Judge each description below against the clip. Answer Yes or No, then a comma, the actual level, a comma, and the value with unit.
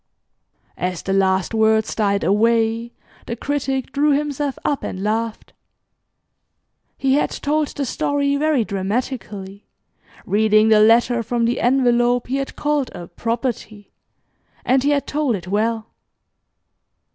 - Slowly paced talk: Yes, slow, 130 wpm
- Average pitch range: Yes, average, 4.2 semitones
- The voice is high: Yes, high, 235 Hz